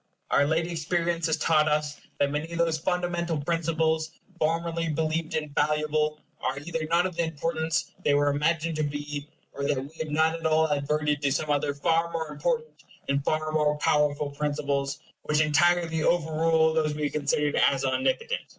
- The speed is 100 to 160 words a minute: No, average, 175 wpm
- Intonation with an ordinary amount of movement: No, narrow, 2.0 semitones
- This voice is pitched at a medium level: Yes, medium, 155 Hz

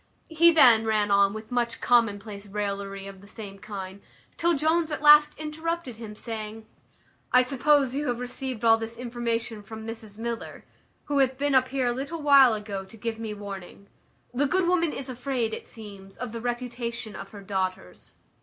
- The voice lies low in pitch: No, high, 230 Hz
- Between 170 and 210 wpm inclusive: Yes, average, 180 wpm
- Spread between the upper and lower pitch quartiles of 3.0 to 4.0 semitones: No, average, 4.4 semitones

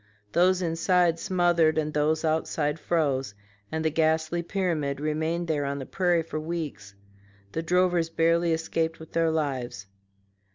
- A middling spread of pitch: No, narrow, 1.9 semitones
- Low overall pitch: No, medium, 160 Hz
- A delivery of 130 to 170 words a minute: Yes, average, 140 wpm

